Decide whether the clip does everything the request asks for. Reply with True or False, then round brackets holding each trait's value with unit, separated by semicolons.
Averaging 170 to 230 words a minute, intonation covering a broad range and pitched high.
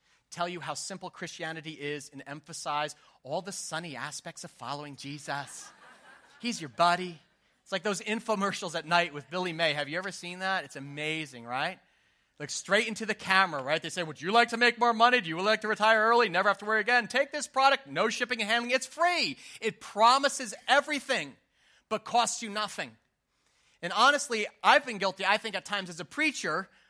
True (200 wpm; 6.2 semitones; 195 Hz)